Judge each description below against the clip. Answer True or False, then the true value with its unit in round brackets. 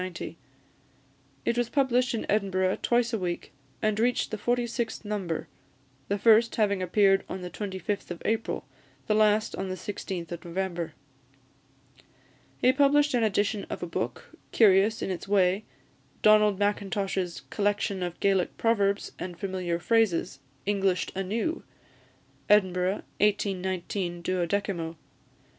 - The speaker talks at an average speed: False (130 wpm)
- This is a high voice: True (200 Hz)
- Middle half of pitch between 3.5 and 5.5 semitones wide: False (2.8 semitones)